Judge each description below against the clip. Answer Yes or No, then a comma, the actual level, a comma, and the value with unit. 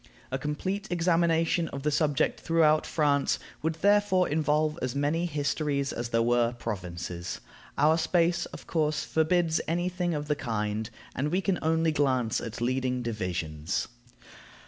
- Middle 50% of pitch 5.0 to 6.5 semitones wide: Yes, average, 5.3 semitones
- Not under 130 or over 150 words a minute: Yes, average, 145 wpm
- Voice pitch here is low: No, medium, 150 Hz